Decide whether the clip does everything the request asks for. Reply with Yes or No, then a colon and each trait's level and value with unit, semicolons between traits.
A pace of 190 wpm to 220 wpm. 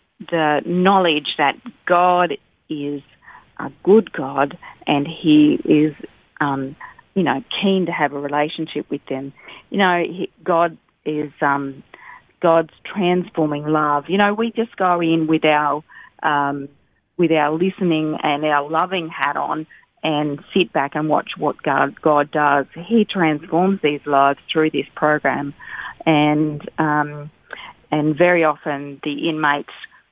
No: average, 140 wpm